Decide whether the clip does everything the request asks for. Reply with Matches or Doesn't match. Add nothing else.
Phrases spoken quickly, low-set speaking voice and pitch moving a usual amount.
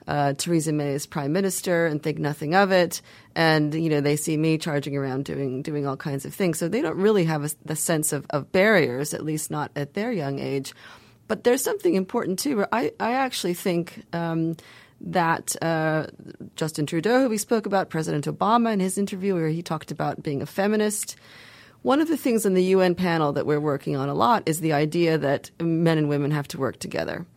Doesn't match